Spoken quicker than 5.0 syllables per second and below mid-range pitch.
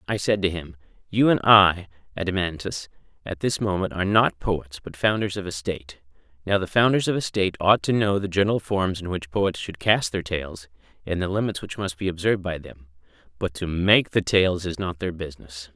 Yes: 5.5 syllables/s; very low, 95 Hz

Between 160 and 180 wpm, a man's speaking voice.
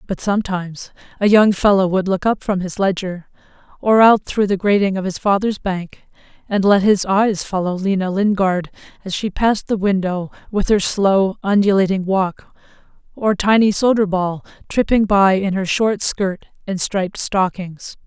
No: average, 165 wpm; female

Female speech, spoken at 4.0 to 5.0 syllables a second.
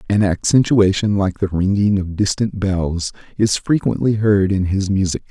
No: male; 4.6 syllables/s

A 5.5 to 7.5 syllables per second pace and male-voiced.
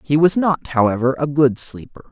No: 5.1 syllables/s; male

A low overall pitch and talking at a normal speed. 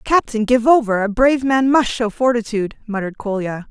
No: high, 230 Hz; average, 180 wpm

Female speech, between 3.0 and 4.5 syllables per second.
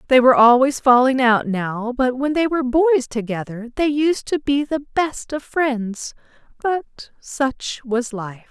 Yes: female; 4.0 syllables/s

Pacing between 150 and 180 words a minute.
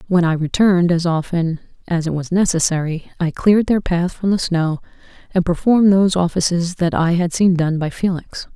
No: average, 190 wpm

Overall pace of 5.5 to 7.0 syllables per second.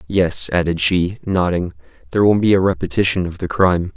Yes: 5.7 syllables/s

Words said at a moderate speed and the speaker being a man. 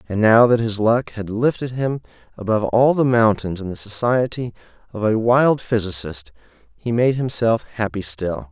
Yes: average, 170 wpm; male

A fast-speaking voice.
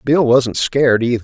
No: average, 195 wpm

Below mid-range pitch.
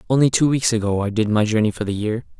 Yes: low, 110 Hz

